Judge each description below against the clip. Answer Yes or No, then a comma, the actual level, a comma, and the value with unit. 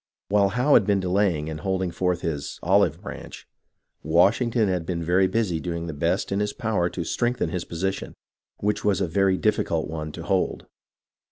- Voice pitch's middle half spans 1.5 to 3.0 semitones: No, average, 3.4 semitones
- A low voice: Yes, very low, 95 Hz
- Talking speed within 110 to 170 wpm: No, average, 190 wpm